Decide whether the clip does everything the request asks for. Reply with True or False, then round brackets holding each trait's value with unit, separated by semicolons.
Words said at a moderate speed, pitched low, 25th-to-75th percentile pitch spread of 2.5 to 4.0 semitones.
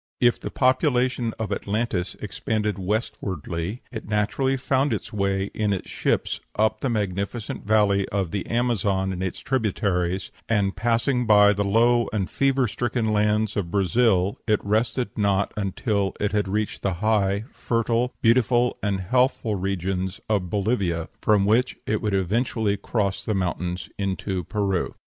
True (150 wpm; 105 Hz; 3.0 semitones)